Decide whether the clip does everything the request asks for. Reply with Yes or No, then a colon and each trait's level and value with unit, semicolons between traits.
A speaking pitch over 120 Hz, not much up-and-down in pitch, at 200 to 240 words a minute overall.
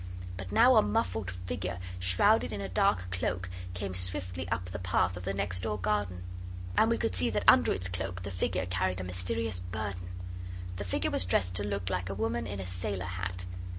No: very low, 90 Hz; narrow, 1.7 semitones; fast, 205 wpm